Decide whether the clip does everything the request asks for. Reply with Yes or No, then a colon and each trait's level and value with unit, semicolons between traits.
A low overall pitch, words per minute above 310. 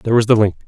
Yes: low, 110 Hz; fast, 355 wpm